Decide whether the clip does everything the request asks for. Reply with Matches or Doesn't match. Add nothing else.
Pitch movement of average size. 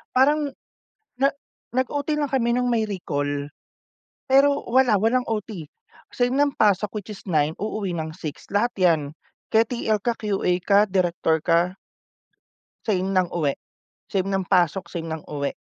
Doesn't match